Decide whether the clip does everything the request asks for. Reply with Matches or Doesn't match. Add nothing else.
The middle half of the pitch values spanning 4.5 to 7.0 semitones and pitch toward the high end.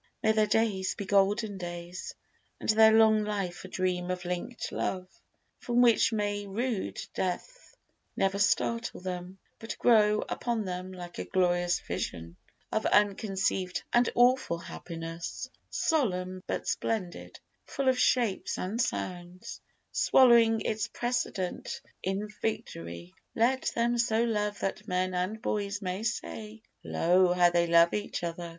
Doesn't match